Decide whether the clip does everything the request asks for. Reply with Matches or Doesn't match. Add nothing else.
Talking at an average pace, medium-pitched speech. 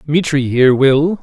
Matches